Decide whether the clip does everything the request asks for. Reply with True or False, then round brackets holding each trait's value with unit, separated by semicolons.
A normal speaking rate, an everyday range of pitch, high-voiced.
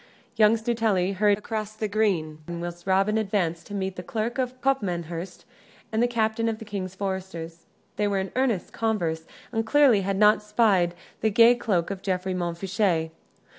True (170 wpm; 3.4 semitones; 200 Hz)